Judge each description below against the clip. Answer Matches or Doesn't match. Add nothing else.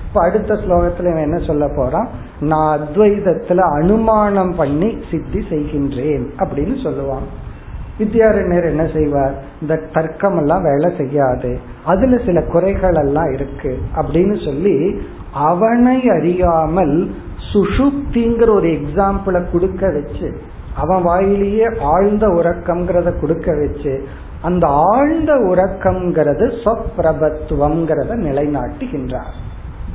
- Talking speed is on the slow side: Doesn't match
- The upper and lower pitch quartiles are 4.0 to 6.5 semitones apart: Matches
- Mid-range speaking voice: Matches